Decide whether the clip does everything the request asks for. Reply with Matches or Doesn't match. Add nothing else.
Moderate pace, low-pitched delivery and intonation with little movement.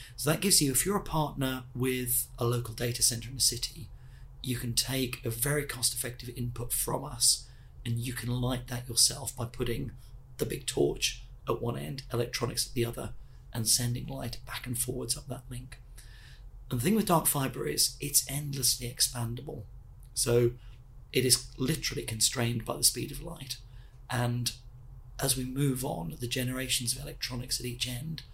Matches